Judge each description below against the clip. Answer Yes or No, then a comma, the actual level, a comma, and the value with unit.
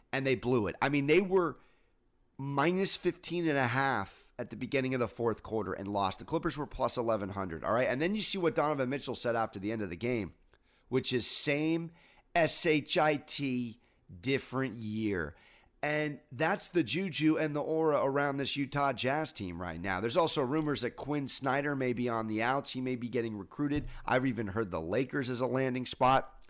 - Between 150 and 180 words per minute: No, average, 200 wpm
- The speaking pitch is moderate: No, low, 130 Hz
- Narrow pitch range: No, average, 4.1 semitones